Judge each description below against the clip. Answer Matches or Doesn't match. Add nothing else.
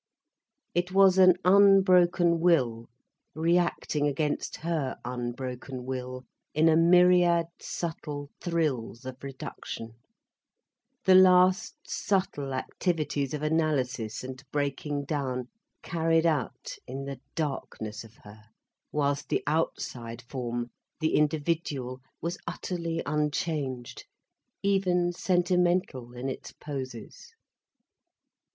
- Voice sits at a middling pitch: Matches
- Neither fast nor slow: Doesn't match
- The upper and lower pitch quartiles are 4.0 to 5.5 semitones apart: Matches